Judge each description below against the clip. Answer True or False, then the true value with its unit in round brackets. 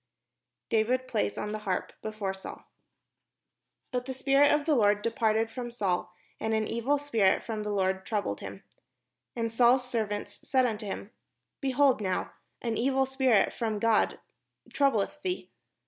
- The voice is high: True (225 Hz)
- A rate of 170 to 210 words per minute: False (160 wpm)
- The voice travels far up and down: False (3.8 semitones)